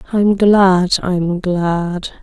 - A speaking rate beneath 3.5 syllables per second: Yes, 2.2 syllables/s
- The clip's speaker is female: Yes, female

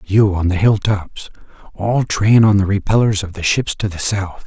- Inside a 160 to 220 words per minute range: Yes, average, 200 wpm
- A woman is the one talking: No, male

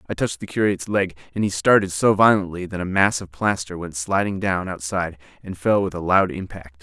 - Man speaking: Yes, male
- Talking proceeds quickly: Yes, fast, 220 wpm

